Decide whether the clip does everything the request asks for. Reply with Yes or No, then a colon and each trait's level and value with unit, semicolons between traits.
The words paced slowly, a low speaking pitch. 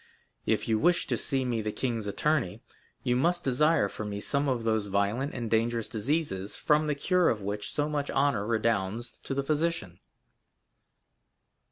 No: average, 170 wpm; low, 120 Hz